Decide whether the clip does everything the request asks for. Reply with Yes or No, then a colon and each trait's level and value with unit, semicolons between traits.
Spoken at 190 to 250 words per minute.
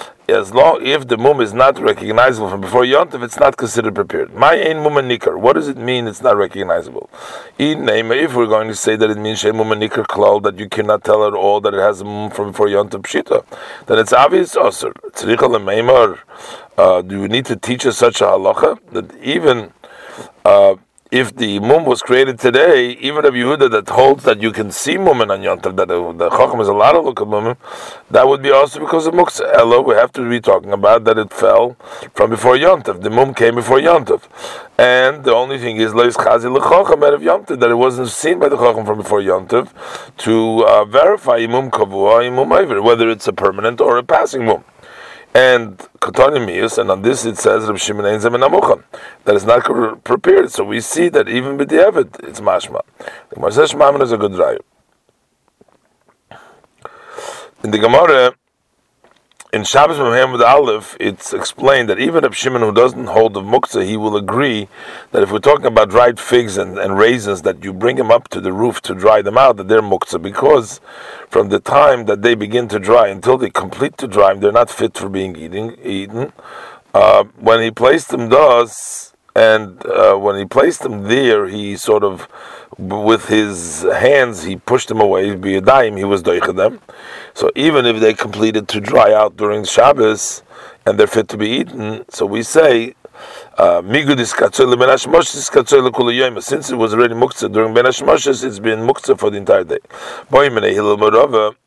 No: average, 180 wpm